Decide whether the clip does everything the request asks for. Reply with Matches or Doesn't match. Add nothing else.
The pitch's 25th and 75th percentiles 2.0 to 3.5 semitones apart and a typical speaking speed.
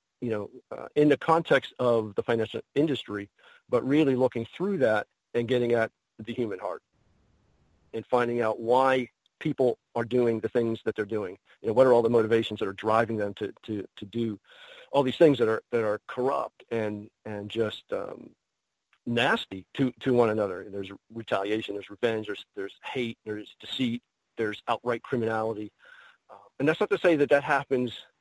Matches